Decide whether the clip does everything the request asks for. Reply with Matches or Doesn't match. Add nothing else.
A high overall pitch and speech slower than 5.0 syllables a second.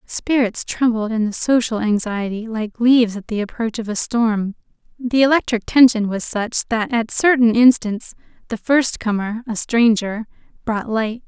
Matches